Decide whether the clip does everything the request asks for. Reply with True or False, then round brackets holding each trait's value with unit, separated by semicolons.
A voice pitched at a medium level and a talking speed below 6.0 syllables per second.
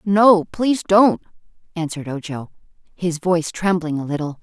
True (175 Hz; 5.1 syllables/s)